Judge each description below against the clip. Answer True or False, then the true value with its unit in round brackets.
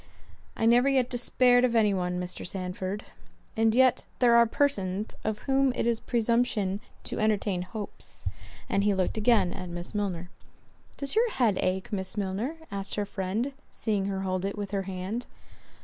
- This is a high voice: True (210 Hz)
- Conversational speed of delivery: True (170 wpm)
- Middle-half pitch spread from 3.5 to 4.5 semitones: True (3.9 semitones)